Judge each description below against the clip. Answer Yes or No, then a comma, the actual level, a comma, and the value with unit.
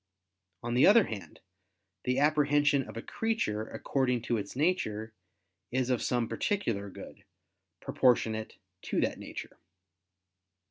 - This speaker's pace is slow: Yes, slow, 125 wpm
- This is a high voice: No, low, 125 Hz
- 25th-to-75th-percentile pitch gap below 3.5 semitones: No, average, 4.8 semitones